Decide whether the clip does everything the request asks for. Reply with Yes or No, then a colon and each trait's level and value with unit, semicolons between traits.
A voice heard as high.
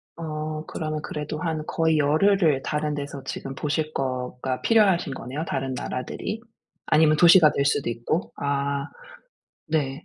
No: medium, 150 Hz